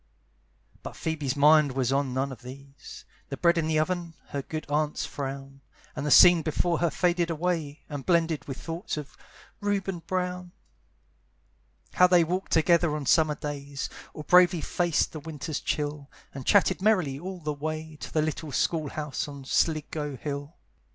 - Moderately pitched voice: Yes, medium, 155 Hz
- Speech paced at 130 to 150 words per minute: No, average, 165 wpm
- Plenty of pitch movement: No, average, 3.3 semitones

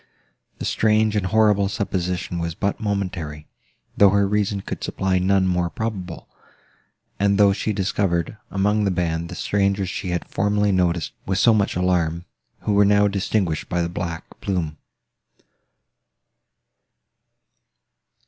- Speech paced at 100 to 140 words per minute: Yes, slow, 135 wpm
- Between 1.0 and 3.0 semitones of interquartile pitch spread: Yes, average, 2.7 semitones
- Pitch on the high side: No, very low, 95 Hz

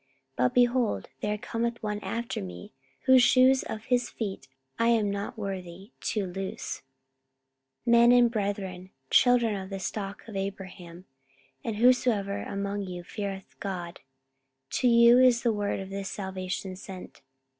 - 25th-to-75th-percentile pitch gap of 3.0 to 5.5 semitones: Yes, average, 3.5 semitones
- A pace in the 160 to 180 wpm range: No, average, 145 wpm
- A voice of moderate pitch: No, high, 205 Hz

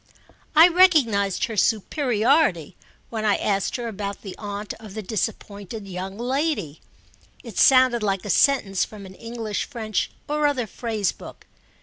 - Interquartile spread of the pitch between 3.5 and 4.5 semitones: Yes, average, 4.1 semitones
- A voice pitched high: Yes, high, 215 Hz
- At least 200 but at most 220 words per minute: No, average, 145 wpm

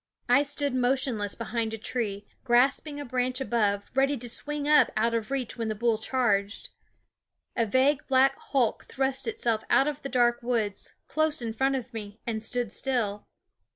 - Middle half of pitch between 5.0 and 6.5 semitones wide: No, average, 3.3 semitones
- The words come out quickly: No, average, 180 wpm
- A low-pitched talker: No, high, 245 Hz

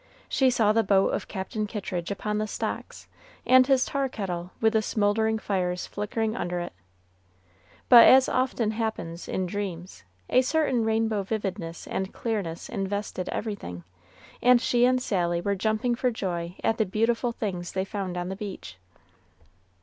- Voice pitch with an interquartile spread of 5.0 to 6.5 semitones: No, average, 3.6 semitones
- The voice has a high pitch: Yes, high, 210 Hz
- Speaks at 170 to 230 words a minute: No, average, 155 wpm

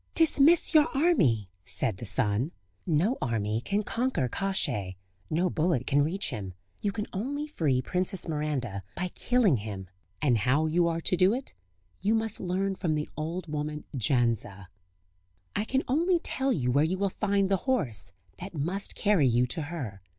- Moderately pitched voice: Yes, medium, 165 Hz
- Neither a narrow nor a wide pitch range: No, wide, 8.3 semitones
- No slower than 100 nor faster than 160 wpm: No, average, 170 wpm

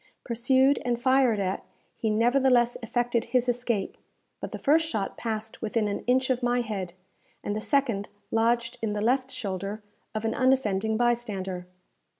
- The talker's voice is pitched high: Yes, high, 235 Hz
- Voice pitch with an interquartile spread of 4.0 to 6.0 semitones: No, average, 2.8 semitones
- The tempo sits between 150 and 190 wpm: Yes, average, 155 wpm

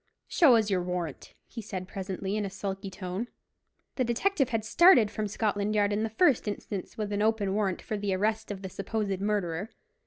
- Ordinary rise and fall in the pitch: No, narrow, 2.3 semitones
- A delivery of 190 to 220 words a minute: Yes, average, 195 wpm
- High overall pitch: Yes, high, 205 Hz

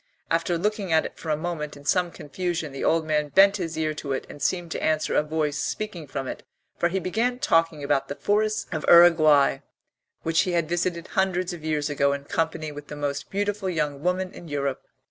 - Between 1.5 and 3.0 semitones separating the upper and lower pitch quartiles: No, average, 3.5 semitones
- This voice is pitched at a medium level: Yes, medium, 165 Hz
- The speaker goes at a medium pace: No, fast, 215 wpm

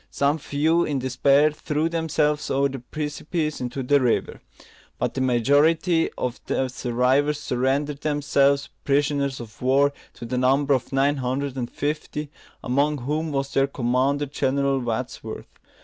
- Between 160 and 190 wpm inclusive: No, average, 145 wpm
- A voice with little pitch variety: Yes, narrow, 2.2 semitones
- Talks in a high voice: No, medium, 140 Hz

